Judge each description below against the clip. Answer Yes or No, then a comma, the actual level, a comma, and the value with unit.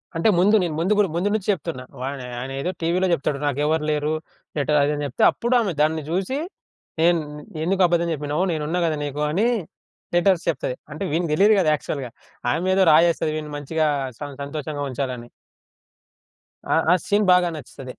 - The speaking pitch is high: No, medium, 160 Hz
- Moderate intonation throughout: Yes, average, 3.6 semitones